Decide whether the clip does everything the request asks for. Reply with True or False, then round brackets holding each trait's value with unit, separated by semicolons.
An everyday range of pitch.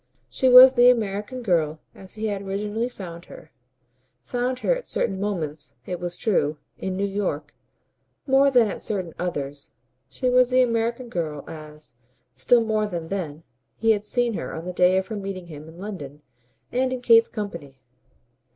False (5.9 semitones)